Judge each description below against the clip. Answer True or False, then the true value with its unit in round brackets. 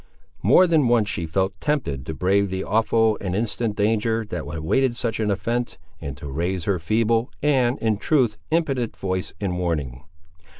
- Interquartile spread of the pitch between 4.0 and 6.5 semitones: True (4.8 semitones)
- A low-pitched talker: True (105 Hz)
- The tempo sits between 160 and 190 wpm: True (170 wpm)